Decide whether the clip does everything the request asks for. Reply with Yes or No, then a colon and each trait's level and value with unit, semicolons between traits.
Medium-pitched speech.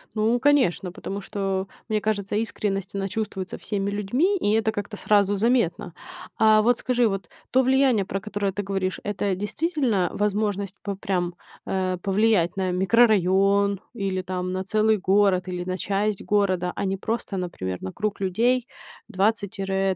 No: high, 200 Hz